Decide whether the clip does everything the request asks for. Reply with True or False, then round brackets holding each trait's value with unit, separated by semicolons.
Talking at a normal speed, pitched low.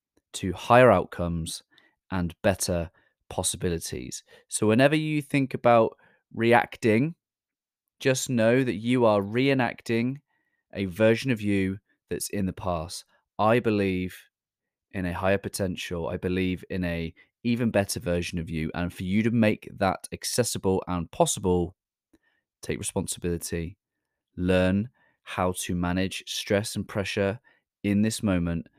False (130 wpm; 100 Hz)